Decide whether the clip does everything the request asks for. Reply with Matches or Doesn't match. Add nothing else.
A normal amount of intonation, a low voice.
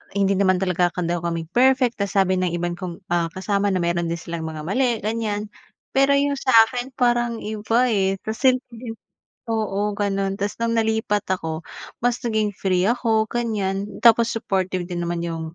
Doesn't match